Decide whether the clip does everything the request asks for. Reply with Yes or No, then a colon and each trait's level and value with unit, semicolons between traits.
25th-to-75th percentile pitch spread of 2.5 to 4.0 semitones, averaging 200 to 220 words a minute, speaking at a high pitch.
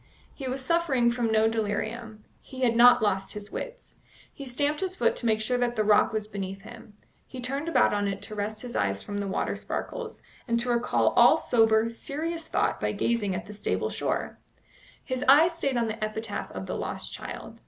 Yes: average, 3.6 semitones; fast, 205 wpm; high, 230 Hz